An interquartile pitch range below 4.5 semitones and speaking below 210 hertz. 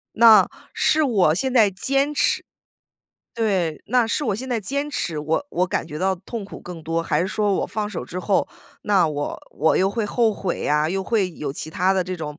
No: average, 5.3 semitones; high, 195 Hz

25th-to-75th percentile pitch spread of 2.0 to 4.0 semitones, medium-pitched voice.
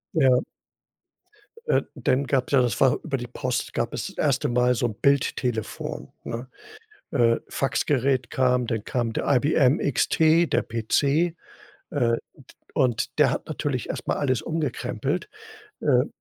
No: average, 2.9 semitones; low, 130 Hz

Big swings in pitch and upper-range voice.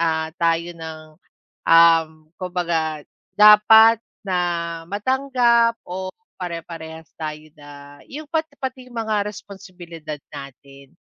No: wide, 5.7 semitones; medium, 175 Hz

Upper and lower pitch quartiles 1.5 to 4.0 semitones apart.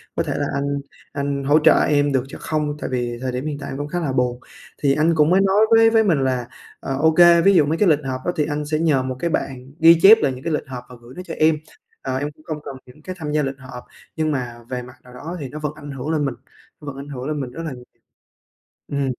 Yes: average, 3.3 semitones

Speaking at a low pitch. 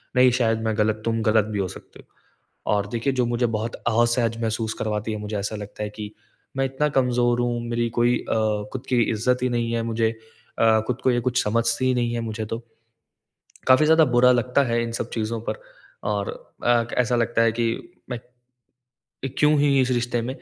Yes: low, 120 Hz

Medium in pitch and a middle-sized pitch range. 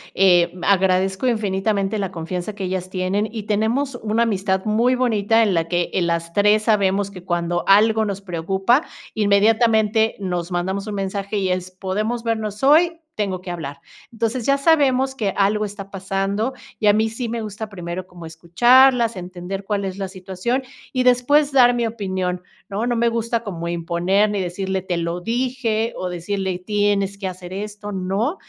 No: high, 200 Hz; average, 3.4 semitones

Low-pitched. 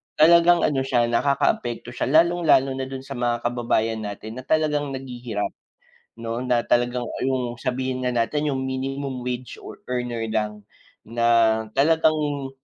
Yes: low, 125 Hz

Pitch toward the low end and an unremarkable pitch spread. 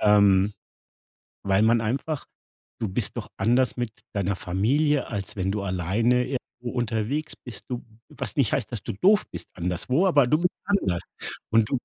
Yes: low, 115 Hz; average, 4.9 semitones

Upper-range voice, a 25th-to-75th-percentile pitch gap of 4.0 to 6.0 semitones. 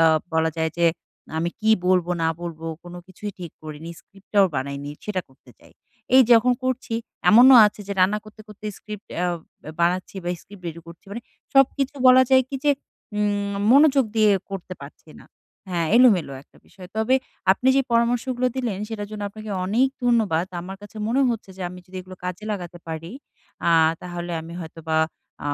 Yes: high, 200 Hz; average, 5.0 semitones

